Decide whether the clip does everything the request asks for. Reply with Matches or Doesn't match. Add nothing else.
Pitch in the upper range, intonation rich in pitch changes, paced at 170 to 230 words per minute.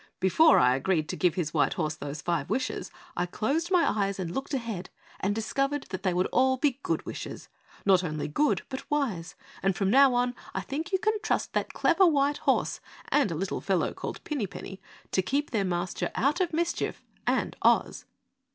Matches